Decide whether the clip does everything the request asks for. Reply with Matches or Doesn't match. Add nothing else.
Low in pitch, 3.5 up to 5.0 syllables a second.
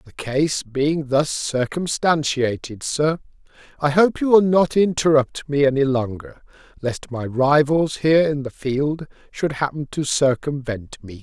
Doesn't match